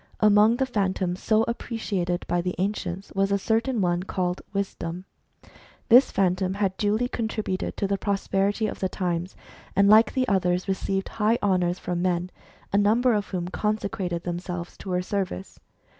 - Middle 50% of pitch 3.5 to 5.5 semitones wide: No, average, 2.8 semitones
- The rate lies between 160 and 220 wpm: Yes, average, 170 wpm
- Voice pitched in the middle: No, high, 195 Hz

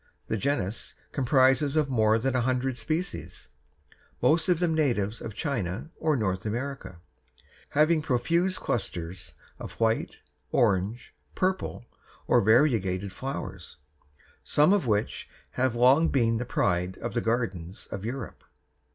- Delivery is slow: Yes, slow, 125 wpm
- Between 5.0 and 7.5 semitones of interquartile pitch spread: Yes, average, 5.3 semitones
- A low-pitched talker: Yes, low, 120 Hz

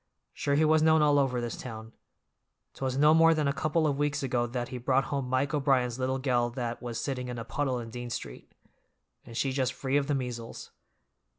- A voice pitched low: Yes, low, 130 Hz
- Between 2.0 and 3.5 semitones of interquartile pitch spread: Yes, average, 2.8 semitones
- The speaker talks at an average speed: No, fast, 215 wpm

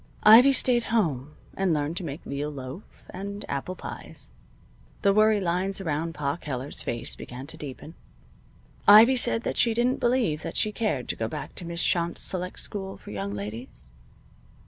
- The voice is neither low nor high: Yes, medium, 170 Hz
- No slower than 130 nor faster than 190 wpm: Yes, average, 170 wpm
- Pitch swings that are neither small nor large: No, wide, 7.2 semitones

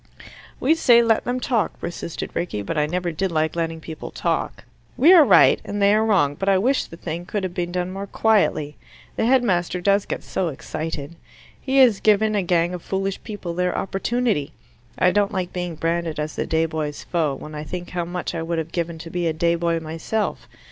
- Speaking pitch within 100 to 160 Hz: No, medium, 175 Hz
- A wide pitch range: No, average, 3.9 semitones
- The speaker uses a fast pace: Yes, fast, 215 wpm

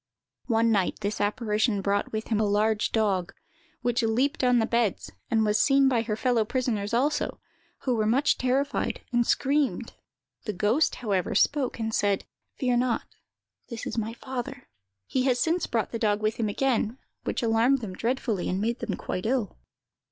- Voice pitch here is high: Yes, high, 230 Hz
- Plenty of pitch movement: No, average, 3.2 semitones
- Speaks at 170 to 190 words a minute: Yes, average, 175 wpm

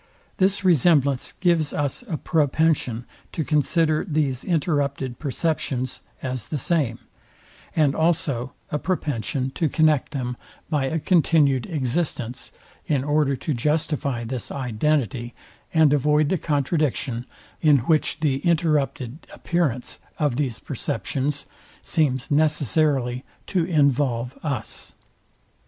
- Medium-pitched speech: Yes, medium, 145 Hz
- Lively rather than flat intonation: No, average, 3.4 semitones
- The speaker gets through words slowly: Yes, slow, 110 wpm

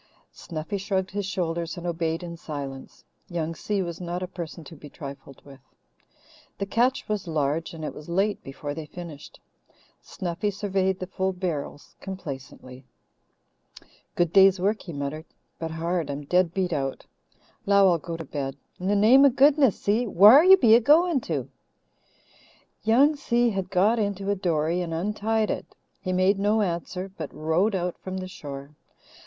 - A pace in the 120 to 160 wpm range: No, average, 170 wpm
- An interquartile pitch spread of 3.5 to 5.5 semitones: Yes, average, 4.0 semitones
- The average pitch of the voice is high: No, medium, 180 Hz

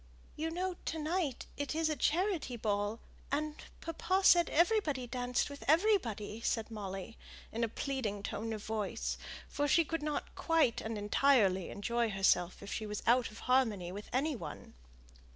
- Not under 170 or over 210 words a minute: No, average, 160 wpm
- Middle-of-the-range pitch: No, high, 245 Hz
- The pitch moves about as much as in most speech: No, wide, 6.7 semitones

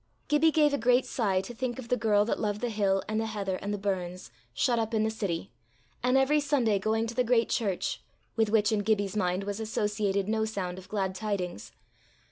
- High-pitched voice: Yes, high, 215 Hz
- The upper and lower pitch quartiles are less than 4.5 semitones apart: Yes, average, 2.9 semitones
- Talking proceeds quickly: Yes, fast, 220 wpm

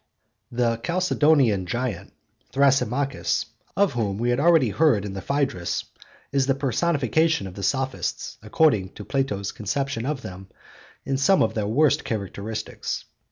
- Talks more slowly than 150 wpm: Yes, average, 140 wpm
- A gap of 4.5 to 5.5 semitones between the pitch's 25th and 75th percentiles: Yes, average, 5.2 semitones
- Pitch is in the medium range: No, low, 125 Hz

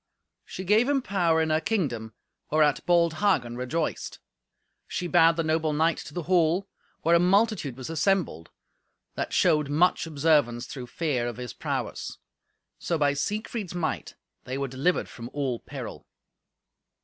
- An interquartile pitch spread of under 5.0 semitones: Yes, average, 4.3 semitones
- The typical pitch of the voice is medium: Yes, medium, 160 Hz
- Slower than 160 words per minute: Yes, average, 150 wpm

